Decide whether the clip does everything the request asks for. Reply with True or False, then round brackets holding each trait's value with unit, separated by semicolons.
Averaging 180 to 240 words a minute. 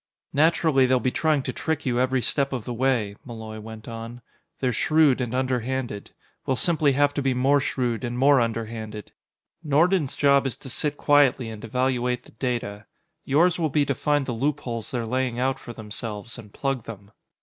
True (185 wpm)